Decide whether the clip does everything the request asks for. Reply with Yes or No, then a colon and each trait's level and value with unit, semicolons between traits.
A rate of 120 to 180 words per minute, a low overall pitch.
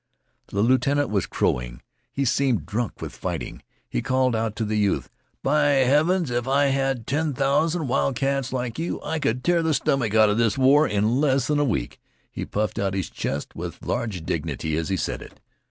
No: average, 190 wpm; low, 130 Hz